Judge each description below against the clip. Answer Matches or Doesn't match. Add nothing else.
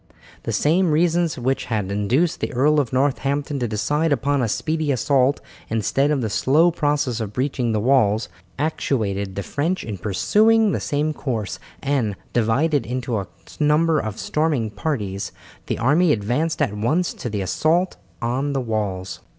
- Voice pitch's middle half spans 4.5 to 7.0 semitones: Matches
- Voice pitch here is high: Doesn't match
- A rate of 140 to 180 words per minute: Matches